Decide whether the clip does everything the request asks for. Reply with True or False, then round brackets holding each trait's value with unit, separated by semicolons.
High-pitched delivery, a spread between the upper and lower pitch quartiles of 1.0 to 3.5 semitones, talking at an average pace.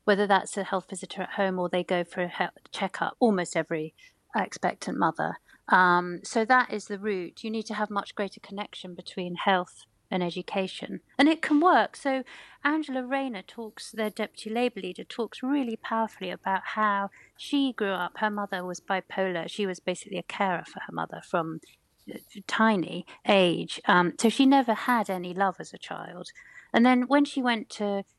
False (205 Hz; 4.7 semitones; 185 wpm)